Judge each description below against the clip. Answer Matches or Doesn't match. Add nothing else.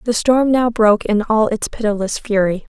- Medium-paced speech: Matches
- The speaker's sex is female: Matches